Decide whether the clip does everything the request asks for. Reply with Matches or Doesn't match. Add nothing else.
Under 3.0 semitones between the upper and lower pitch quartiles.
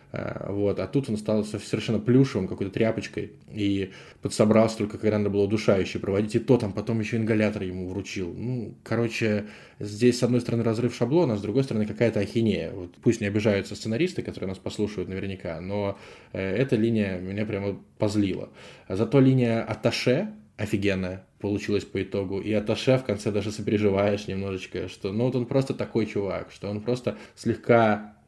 Matches